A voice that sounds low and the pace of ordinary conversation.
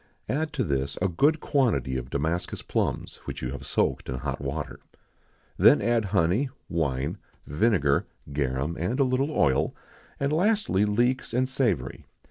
Yes: very low, 90 Hz; average, 150 wpm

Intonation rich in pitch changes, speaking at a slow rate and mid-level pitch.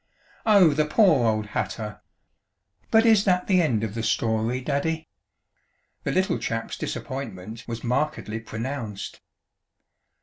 No: wide, 6.4 semitones; slow, 125 wpm; low, 125 Hz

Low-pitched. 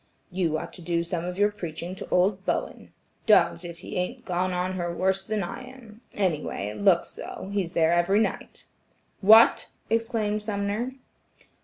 No: medium, 185 Hz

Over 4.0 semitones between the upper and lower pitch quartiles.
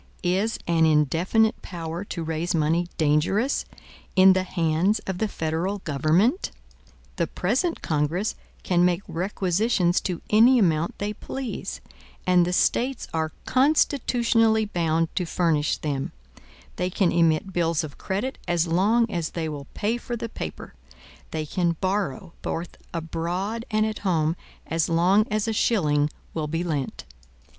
Yes: average, 4.5 semitones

